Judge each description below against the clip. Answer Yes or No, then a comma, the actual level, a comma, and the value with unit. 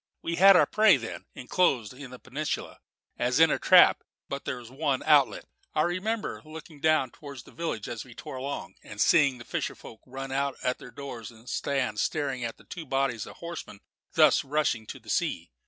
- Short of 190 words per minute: No, fast, 205 wpm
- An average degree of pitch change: Yes, average, 3.9 semitones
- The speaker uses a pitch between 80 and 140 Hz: Yes, low, 135 Hz